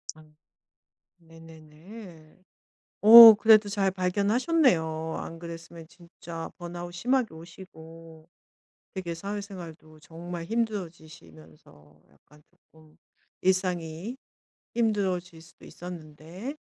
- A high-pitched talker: No, medium, 170 Hz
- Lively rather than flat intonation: No, average, 3.8 semitones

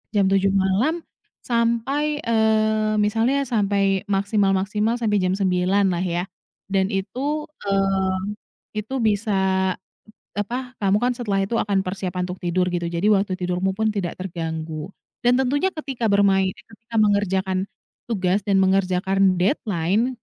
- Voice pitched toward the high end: Yes, high, 195 Hz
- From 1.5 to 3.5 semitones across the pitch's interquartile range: Yes, average, 2.9 semitones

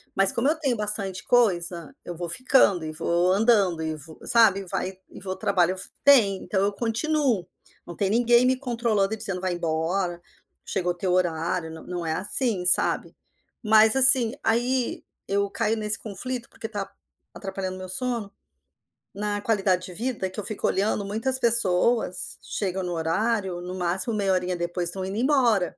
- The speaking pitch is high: Yes, high, 195 Hz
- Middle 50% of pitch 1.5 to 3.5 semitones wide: No, average, 4.2 semitones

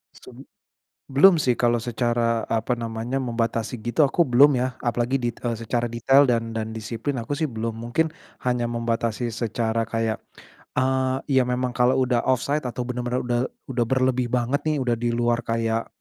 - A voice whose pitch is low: Yes, low, 120 Hz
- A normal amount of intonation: No, narrow, 2.0 semitones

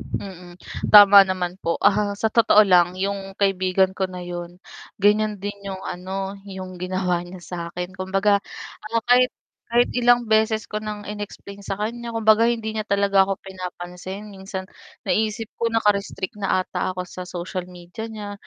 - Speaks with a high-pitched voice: Yes, high, 195 Hz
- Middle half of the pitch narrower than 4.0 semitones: Yes, narrow, 2.5 semitones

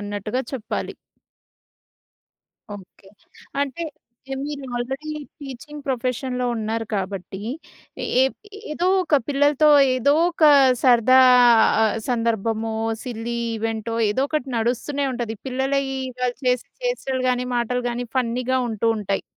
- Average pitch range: Yes, average, 3.2 semitones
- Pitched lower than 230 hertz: No, very high, 250 Hz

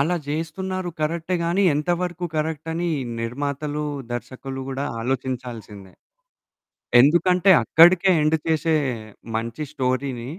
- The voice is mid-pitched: Yes, medium, 150 Hz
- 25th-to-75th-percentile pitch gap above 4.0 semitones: Yes, average, 4.7 semitones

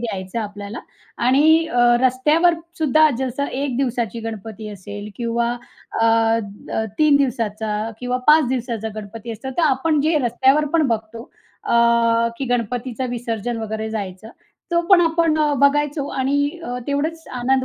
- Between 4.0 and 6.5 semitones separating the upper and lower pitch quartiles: Yes, average, 4.3 semitones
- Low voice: No, high, 245 Hz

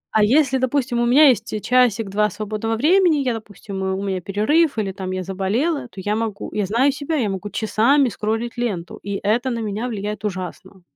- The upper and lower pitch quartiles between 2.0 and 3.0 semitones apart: No, average, 4.2 semitones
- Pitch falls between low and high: No, high, 220 Hz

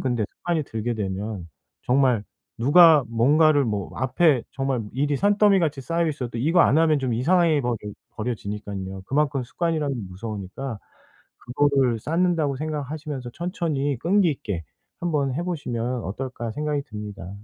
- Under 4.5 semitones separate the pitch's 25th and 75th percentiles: No, average, 5.3 semitones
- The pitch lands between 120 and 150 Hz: Yes, low, 135 Hz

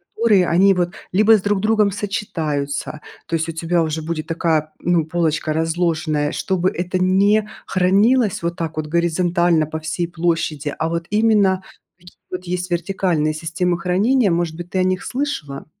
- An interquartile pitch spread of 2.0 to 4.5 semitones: Yes, average, 2.9 semitones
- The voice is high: No, medium, 175 Hz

